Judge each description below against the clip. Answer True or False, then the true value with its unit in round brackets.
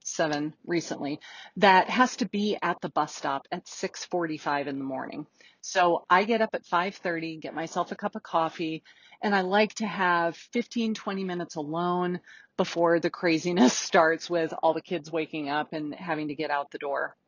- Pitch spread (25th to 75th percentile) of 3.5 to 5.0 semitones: False (3.1 semitones)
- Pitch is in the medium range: True (175 Hz)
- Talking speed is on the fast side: False (185 wpm)